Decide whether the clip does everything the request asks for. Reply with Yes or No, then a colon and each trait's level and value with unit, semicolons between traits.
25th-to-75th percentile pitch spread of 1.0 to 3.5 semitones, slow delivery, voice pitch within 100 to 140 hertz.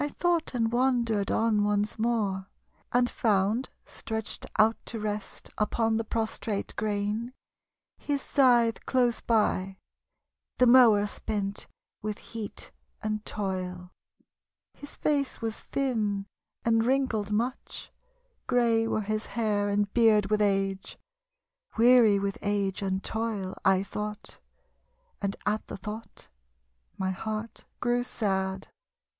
No: narrow, 2.5 semitones; slow, 120 wpm; high, 215 Hz